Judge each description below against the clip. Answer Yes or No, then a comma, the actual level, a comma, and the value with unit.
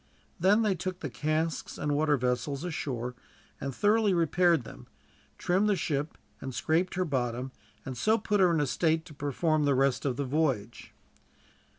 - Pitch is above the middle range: No, medium, 155 Hz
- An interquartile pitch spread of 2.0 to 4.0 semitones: No, average, 4.8 semitones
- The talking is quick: No, average, 175 wpm